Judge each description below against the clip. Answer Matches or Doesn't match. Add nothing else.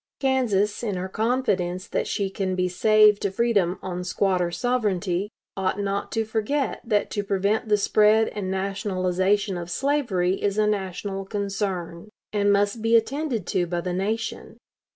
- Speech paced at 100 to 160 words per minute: Matches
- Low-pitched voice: Doesn't match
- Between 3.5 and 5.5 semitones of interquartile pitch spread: Doesn't match